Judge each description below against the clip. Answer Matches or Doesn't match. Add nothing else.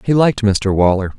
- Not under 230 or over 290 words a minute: Doesn't match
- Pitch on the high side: Doesn't match